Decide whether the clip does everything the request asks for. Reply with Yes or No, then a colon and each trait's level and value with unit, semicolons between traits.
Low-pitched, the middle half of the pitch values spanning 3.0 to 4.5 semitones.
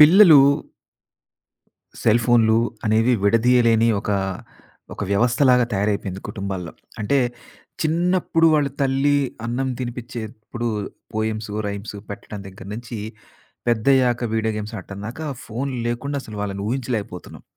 Yes: low, 115 Hz; average, 3.7 semitones